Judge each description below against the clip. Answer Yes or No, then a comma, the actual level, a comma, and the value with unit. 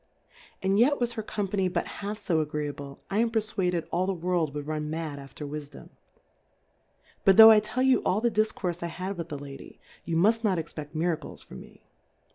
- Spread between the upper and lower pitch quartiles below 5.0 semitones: No, wide, 5.5 semitones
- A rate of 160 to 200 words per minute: Yes, average, 190 wpm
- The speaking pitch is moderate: Yes, medium, 180 Hz